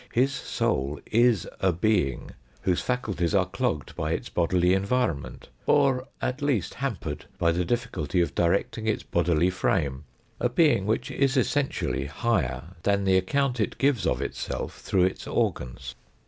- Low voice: Yes, very low, 95 Hz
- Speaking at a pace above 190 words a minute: No, average, 150 wpm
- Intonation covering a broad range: Yes, wide, 6.7 semitones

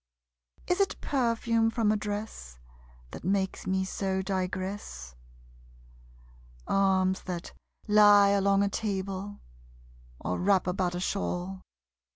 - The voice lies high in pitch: Yes, high, 195 Hz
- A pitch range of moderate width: No, narrow, 1.7 semitones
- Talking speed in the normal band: No, slow, 110 wpm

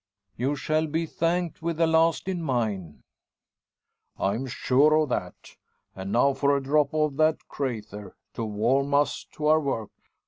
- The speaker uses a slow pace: No, average, 160 wpm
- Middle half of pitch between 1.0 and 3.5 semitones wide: No, average, 4.6 semitones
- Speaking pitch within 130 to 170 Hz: Yes, medium, 140 Hz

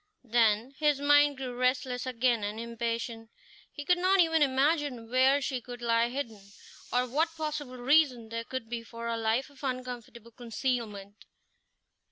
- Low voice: No, very high, 250 Hz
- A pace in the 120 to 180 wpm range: Yes, average, 155 wpm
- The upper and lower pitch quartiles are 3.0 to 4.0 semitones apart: Yes, average, 3.5 semitones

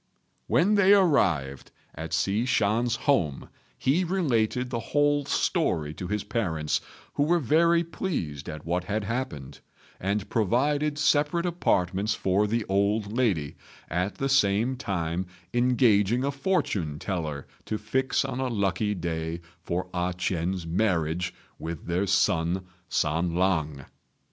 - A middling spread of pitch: No, wide, 7.3 semitones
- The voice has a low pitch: Yes, low, 100 Hz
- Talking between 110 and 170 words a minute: Yes, slow, 135 wpm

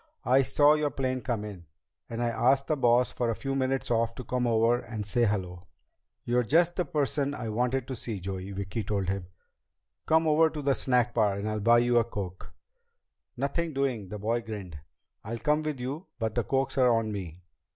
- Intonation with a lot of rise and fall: No, average, 4.2 semitones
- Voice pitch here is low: Yes, low, 120 Hz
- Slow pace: No, fast, 205 wpm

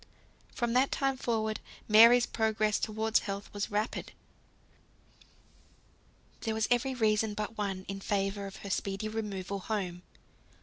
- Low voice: No, high, 215 Hz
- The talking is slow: Yes, slow, 130 wpm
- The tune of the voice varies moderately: No, narrow, 2.0 semitones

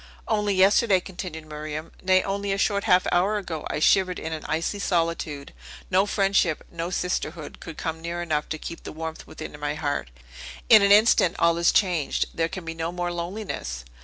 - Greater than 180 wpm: Yes, average, 190 wpm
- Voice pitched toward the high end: No, medium, 175 Hz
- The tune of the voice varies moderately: Yes, average, 3.4 semitones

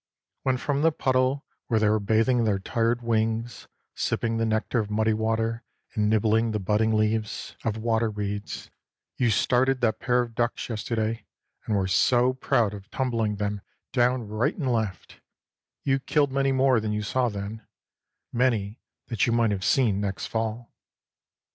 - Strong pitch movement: No, narrow, 2.4 semitones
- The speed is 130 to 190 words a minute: Yes, average, 165 wpm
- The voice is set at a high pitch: No, low, 115 Hz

